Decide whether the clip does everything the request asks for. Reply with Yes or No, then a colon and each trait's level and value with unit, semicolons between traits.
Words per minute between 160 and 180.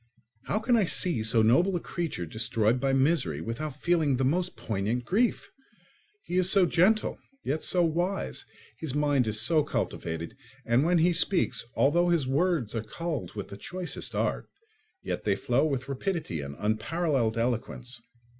Yes: average, 165 wpm